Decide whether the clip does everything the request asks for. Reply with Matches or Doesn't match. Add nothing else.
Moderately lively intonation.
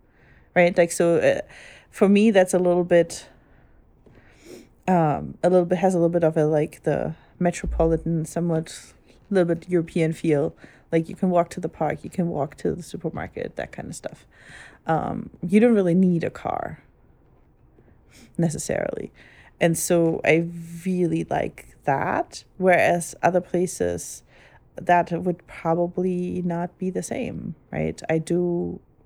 Doesn't match